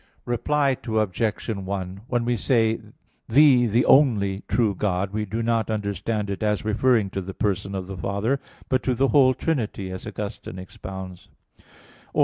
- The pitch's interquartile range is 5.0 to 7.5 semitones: No, average, 3.8 semitones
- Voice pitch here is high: No, low, 105 Hz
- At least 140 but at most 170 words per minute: Yes, average, 165 wpm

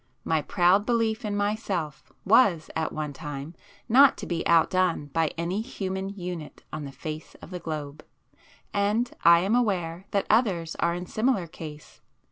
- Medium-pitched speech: Yes, medium, 180 Hz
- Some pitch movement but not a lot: Yes, average, 4.4 semitones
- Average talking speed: Yes, average, 160 wpm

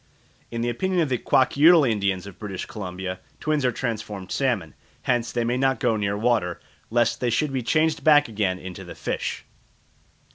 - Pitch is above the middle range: No, low, 120 Hz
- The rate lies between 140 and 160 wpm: No, average, 180 wpm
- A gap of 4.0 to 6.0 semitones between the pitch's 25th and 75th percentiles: Yes, average, 5.0 semitones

